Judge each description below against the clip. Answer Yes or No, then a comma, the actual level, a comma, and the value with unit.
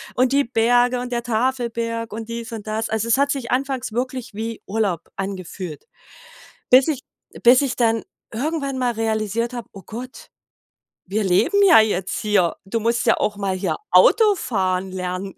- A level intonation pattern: No, average, 3.4 semitones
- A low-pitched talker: No, high, 230 Hz